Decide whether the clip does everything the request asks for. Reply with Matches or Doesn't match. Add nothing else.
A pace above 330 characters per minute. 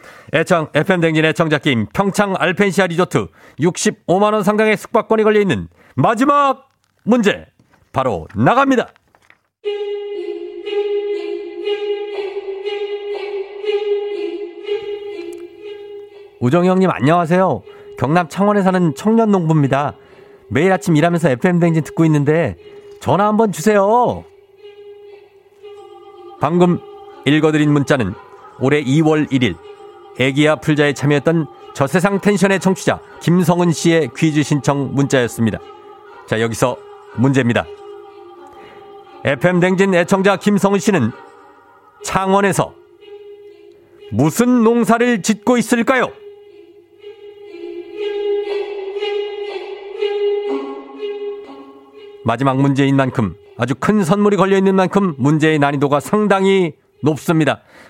Doesn't match